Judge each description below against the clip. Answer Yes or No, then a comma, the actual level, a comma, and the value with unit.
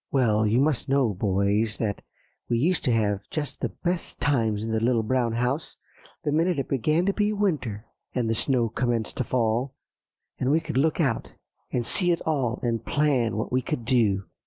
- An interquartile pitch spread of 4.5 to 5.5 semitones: Yes, average, 4.8 semitones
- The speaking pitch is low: Yes, low, 125 Hz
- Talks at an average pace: Yes, average, 195 wpm